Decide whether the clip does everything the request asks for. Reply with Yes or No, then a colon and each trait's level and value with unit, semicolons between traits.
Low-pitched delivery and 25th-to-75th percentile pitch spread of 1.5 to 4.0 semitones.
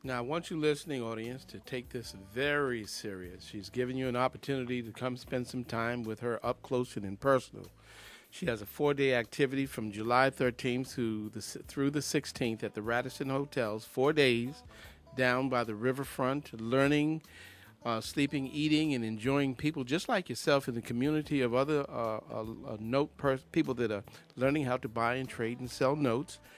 Yes: low, 130 Hz; average, 3.1 semitones